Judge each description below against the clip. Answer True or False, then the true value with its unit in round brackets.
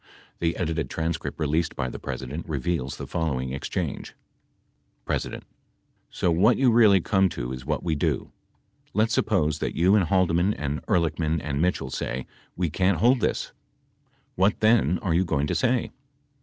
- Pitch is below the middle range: True (85 Hz)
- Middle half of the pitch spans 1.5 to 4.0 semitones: False (4.4 semitones)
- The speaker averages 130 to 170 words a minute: True (165 wpm)